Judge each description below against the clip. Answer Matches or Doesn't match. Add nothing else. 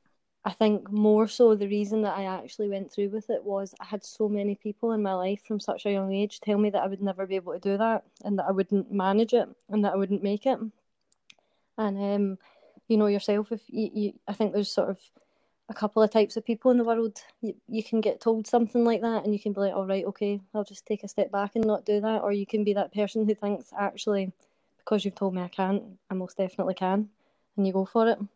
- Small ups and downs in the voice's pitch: Matches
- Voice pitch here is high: Matches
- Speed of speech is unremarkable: Doesn't match